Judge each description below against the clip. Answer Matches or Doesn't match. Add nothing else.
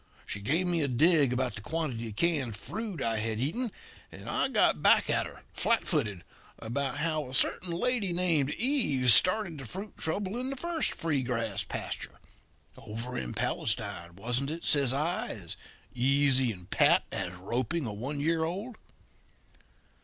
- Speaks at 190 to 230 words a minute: Doesn't match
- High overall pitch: Doesn't match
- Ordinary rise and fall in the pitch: Doesn't match